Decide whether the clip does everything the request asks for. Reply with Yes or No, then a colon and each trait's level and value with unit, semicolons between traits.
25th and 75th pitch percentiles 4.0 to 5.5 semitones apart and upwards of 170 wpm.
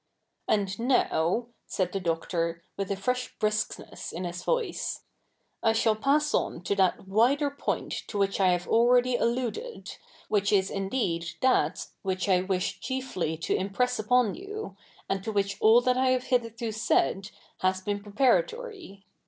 No: average, 4.8 semitones; average, 160 wpm